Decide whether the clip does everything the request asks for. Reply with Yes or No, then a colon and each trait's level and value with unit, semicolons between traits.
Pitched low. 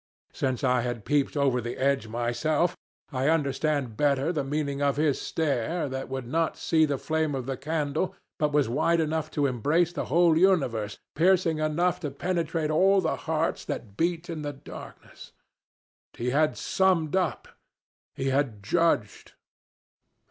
No: medium, 150 Hz